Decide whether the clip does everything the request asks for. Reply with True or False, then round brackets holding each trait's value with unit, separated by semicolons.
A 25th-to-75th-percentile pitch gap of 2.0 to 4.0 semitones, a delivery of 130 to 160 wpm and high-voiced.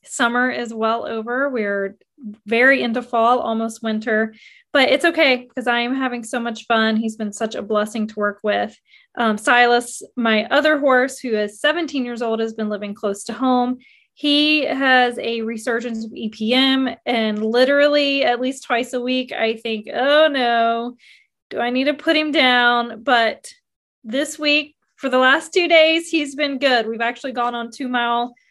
False (3.5 semitones; 180 wpm; 245 Hz)